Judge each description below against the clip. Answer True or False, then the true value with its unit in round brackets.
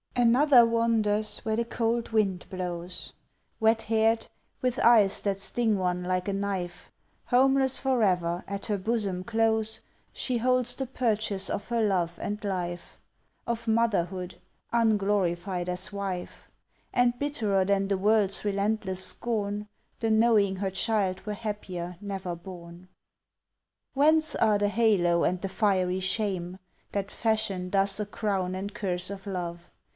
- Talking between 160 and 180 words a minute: False (140 wpm)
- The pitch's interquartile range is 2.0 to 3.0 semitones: False (3.4 semitones)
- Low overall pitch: False (205 Hz)